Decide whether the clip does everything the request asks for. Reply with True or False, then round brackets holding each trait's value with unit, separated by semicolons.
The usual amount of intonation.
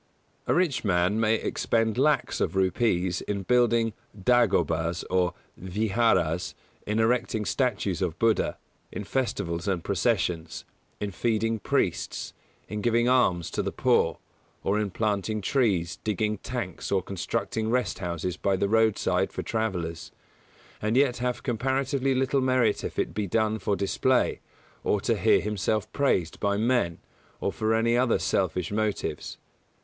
True (4.1 semitones)